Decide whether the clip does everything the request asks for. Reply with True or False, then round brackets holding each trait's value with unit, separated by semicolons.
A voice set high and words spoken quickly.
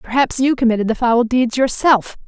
False (245 Hz; 185 wpm)